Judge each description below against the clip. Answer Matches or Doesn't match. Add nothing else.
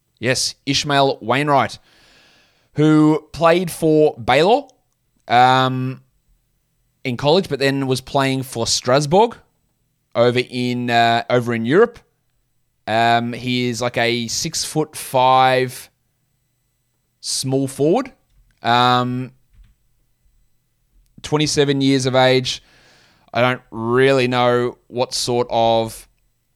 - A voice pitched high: Doesn't match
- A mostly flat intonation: Matches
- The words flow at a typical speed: Doesn't match